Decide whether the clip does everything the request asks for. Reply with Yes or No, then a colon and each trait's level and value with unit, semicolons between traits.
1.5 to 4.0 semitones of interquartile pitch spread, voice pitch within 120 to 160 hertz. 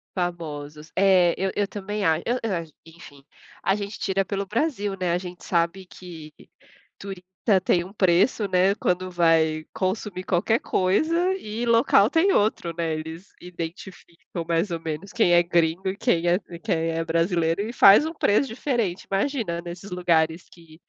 No: average, 3.2 semitones; medium, 180 Hz